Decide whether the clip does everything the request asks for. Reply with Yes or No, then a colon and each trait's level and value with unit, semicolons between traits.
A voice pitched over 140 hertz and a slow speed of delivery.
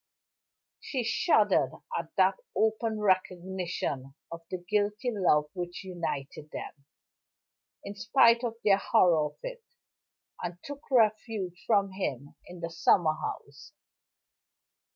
Yes: high, 190 Hz; slow, 115 wpm